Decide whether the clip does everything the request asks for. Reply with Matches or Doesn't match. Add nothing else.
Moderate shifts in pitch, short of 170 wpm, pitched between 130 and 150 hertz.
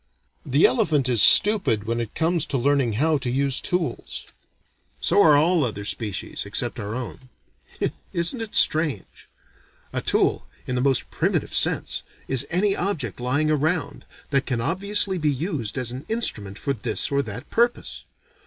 Doesn't match